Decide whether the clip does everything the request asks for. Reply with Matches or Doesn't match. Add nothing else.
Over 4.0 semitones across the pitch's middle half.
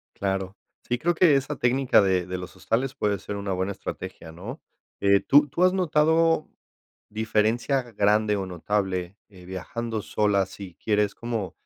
Matches